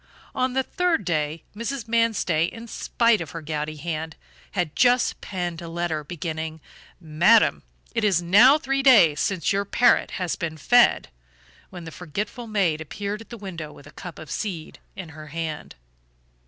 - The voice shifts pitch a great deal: Yes, wide, 6.1 semitones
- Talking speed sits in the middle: Yes, average, 170 wpm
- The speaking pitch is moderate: Yes, medium, 175 Hz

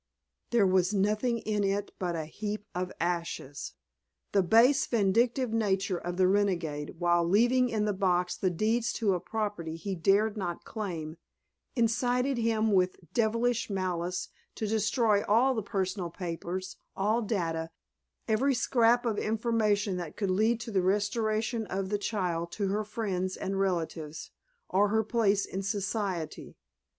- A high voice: Yes, high, 200 Hz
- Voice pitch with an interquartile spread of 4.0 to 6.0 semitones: No, average, 3.4 semitones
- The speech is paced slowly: No, average, 150 wpm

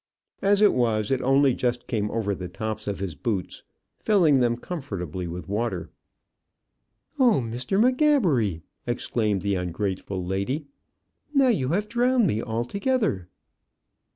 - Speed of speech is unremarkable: No, slow, 130 wpm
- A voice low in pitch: Yes, low, 120 Hz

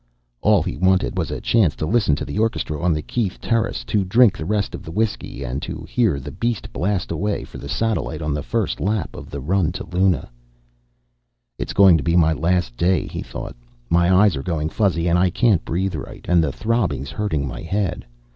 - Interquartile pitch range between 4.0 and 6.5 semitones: Yes, average, 4.7 semitones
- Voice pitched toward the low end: Yes, very low, 90 Hz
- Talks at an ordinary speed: No, fast, 215 wpm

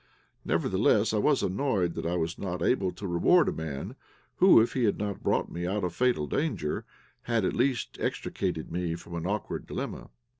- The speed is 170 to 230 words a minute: Yes, average, 190 wpm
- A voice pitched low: Yes, very low, 95 Hz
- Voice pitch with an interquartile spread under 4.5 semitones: No, average, 5.2 semitones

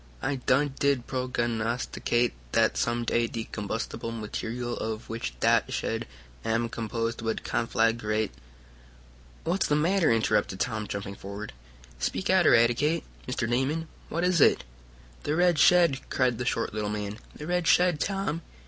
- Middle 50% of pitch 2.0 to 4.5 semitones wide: No, average, 5.1 semitones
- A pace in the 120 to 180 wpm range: Yes, average, 150 wpm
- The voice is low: Yes, low, 120 Hz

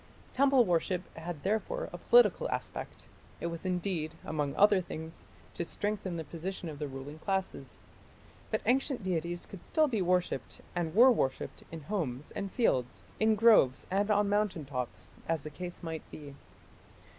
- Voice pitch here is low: No, medium, 175 Hz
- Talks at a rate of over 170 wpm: No, average, 160 wpm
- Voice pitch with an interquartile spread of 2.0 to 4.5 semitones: No, average, 4.9 semitones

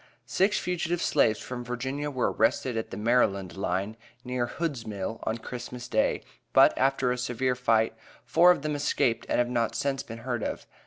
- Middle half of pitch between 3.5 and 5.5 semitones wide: No, average, 3.1 semitones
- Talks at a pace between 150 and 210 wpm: Yes, average, 180 wpm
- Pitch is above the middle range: No, low, 125 Hz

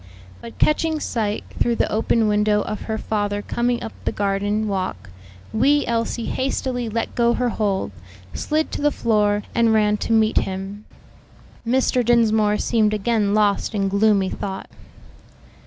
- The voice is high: Yes, high, 215 Hz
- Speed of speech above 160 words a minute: No, average, 150 wpm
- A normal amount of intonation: No, narrow, 2.3 semitones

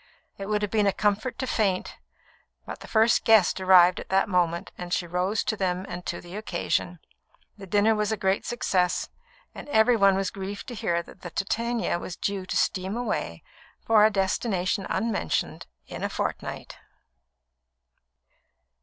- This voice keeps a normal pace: Yes, average, 170 wpm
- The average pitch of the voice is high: Yes, high, 195 Hz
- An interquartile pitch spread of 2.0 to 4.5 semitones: Yes, average, 2.9 semitones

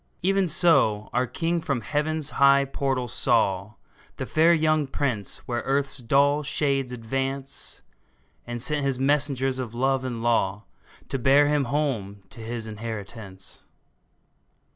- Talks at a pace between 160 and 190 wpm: No, slow, 135 wpm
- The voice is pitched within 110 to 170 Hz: Yes, low, 135 Hz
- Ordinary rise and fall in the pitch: Yes, average, 3.8 semitones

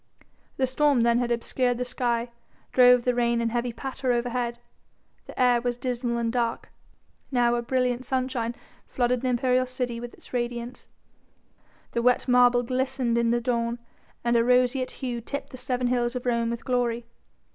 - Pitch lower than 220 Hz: No, high, 245 Hz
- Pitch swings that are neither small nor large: No, narrow, 1.0 semitones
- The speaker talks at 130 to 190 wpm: Yes, average, 170 wpm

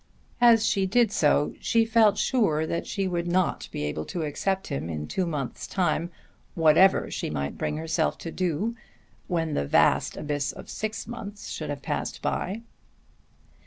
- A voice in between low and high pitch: Yes, medium, 175 Hz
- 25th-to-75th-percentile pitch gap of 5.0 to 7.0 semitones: Yes, average, 5.3 semitones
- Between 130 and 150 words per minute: No, average, 165 wpm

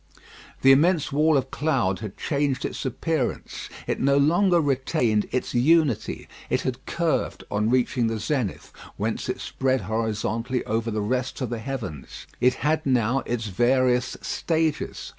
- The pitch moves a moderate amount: Yes, average, 4.0 semitones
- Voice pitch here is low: Yes, low, 130 Hz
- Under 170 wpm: Yes, average, 150 wpm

